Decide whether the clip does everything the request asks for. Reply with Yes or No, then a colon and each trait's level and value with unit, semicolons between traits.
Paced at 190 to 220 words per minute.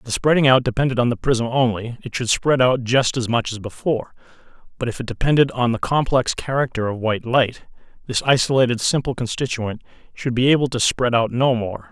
Yes: fast, 205 wpm